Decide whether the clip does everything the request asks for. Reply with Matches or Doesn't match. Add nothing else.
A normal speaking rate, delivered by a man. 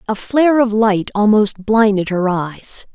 Doesn't match